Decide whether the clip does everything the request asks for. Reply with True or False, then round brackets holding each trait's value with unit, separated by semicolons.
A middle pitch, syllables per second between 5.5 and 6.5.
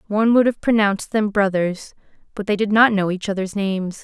False (205 Hz; 5.8 syllables/s)